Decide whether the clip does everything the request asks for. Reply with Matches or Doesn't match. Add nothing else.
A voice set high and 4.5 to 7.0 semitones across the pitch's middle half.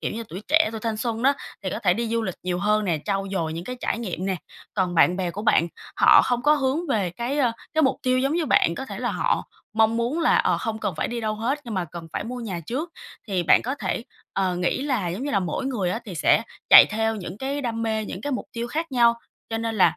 Matches